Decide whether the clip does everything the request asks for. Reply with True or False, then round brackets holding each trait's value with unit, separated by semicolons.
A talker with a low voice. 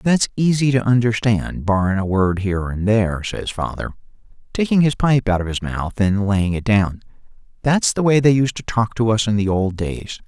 True (110 Hz)